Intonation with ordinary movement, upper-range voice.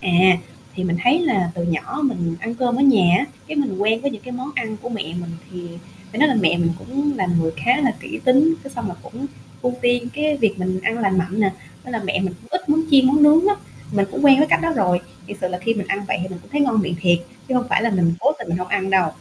No: wide, 6.5 semitones; high, 220 Hz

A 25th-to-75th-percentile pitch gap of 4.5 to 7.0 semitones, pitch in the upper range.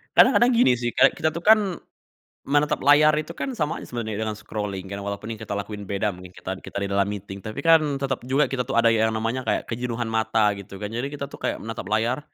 No: average, 5.2 semitones; low, 115 Hz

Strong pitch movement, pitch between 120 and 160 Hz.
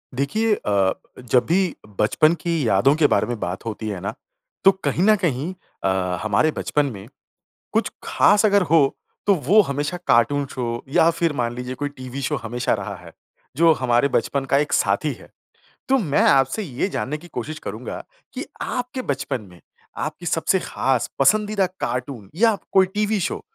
Yes: wide, 6.8 semitones; medium, 140 Hz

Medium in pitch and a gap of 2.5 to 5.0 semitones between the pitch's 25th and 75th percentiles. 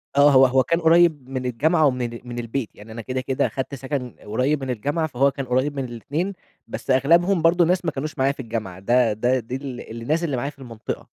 No: low, 130 Hz; average, 3.4 semitones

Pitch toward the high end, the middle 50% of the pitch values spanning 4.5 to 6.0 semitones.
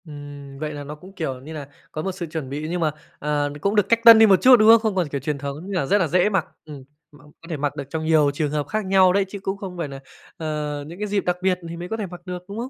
No: medium, 165 Hz; average, 4.8 semitones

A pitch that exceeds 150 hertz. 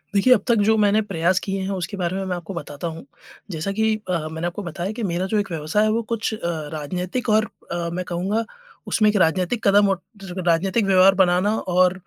Yes: high, 190 Hz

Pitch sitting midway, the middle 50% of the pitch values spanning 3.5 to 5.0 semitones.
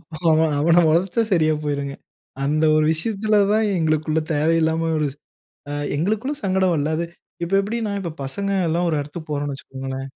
Yes: medium, 160 Hz; average, 4.0 semitones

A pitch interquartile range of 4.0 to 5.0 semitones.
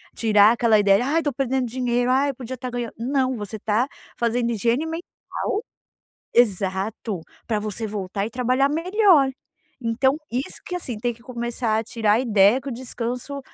No: average, 3.3 semitones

